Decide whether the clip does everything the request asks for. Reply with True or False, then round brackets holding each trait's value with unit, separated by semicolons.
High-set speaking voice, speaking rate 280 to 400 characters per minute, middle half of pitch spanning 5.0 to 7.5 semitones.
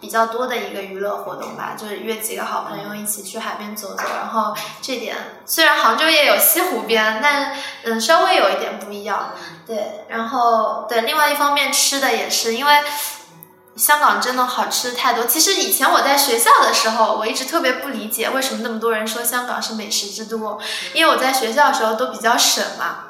False (230 Hz; 310 characters per minute; 4.5 semitones)